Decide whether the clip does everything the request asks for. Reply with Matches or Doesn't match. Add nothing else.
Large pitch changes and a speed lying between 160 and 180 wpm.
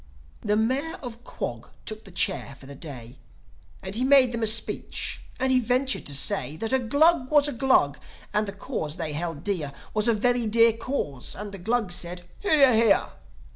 Doesn't match